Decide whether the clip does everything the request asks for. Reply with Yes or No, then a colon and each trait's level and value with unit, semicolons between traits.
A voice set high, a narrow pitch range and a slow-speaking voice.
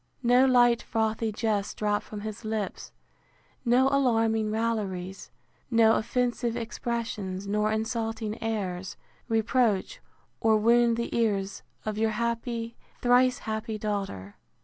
Yes: high, 225 Hz; narrow, 1.8 semitones; slow, 115 wpm